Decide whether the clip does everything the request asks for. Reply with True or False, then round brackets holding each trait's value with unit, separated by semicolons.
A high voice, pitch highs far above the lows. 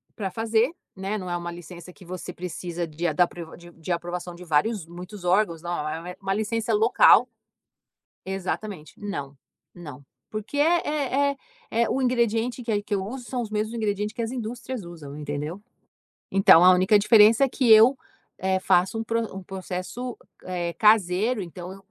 False (195 Hz; 4.3 semitones)